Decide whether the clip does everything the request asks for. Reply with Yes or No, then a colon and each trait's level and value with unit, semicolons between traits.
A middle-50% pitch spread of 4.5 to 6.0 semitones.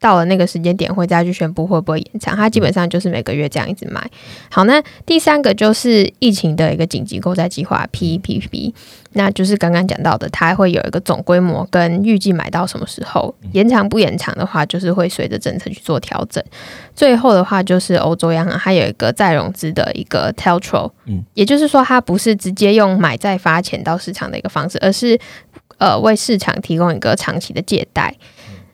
No: average, 3.6 semitones